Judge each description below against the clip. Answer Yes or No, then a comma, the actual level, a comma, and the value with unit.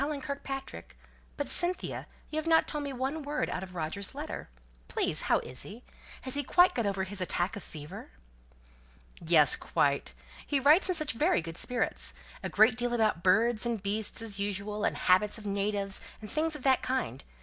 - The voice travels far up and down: Yes, wide, 6.4 semitones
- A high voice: Yes, high, 215 Hz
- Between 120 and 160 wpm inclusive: No, average, 170 wpm